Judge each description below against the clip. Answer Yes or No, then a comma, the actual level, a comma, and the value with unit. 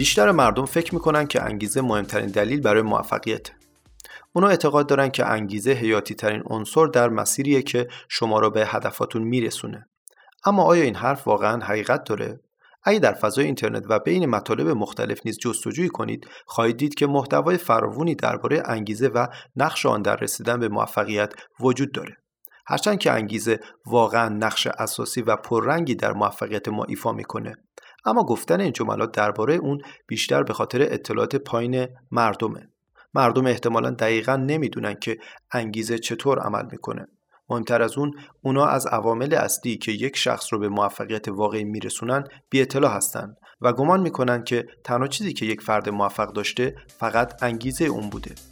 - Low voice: Yes, low, 120 Hz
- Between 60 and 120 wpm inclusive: No, fast, 155 wpm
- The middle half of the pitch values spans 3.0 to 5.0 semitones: Yes, average, 4.0 semitones